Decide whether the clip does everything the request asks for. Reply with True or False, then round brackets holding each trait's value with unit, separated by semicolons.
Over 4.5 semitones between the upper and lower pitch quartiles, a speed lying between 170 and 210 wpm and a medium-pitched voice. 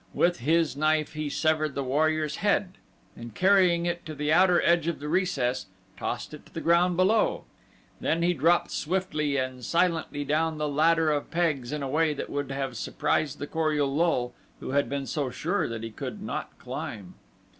False (3.4 semitones; 190 wpm; 155 Hz)